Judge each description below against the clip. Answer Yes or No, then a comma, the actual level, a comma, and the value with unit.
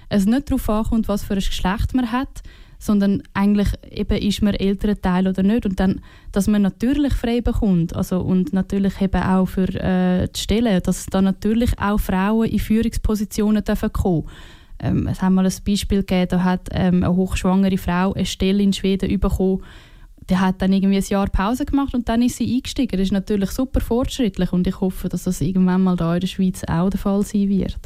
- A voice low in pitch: No, high, 195 Hz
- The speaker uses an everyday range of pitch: No, narrow, 2.3 semitones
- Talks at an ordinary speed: No, fast, 205 wpm